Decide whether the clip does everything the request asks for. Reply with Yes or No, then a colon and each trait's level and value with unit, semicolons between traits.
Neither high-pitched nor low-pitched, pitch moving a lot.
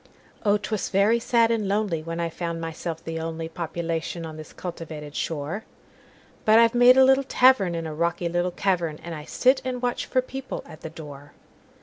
Yes: medium, 170 Hz; wide, 5.8 semitones